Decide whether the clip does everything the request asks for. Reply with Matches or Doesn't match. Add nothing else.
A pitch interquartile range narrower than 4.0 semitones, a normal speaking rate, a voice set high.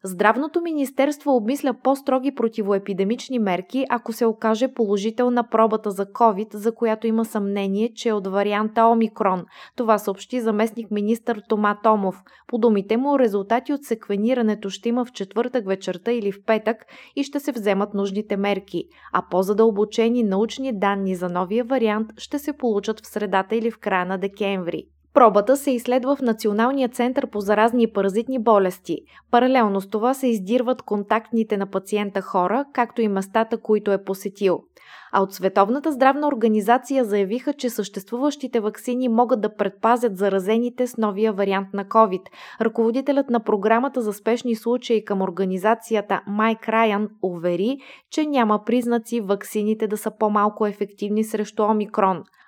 Matches